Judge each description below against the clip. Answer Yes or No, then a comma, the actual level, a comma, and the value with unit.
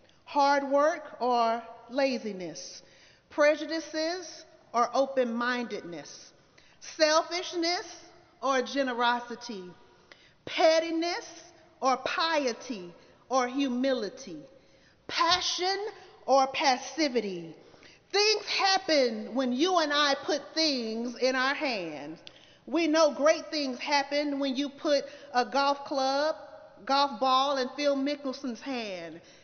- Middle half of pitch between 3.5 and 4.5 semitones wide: Yes, average, 4.2 semitones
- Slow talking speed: Yes, slow, 95 wpm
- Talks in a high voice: Yes, very high, 280 Hz